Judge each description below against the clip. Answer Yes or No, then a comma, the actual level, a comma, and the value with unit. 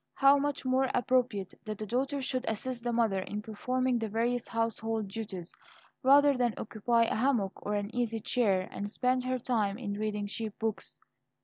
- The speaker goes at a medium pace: Yes, average, 180 wpm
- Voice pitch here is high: Yes, high, 230 Hz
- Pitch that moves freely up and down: No, average, 3.4 semitones